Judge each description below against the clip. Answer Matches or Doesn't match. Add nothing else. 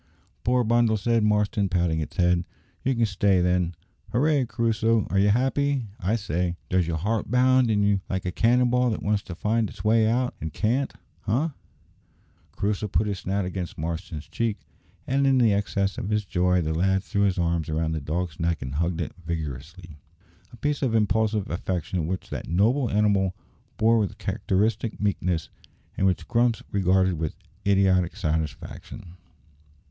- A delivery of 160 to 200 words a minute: Matches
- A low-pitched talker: Matches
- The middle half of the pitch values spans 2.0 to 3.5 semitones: Doesn't match